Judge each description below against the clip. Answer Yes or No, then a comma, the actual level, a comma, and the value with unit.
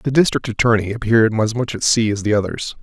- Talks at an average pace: No, fast, 235 wpm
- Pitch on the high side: No, low, 115 Hz